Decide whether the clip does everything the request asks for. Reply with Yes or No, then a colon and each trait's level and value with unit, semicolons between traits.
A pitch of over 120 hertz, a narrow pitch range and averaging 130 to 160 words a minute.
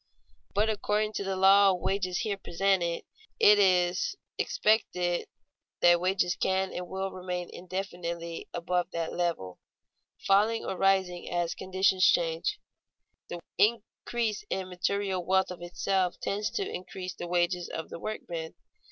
Yes: medium, 185 Hz; narrow, 2.1 semitones; average, 145 wpm